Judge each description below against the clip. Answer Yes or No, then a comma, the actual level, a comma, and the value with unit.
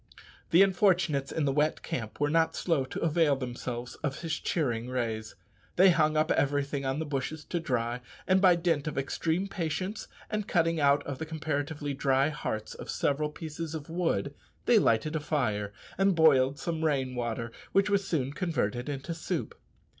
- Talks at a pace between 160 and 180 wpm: Yes, average, 175 wpm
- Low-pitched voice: No, medium, 150 Hz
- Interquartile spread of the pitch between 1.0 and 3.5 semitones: No, average, 3.9 semitones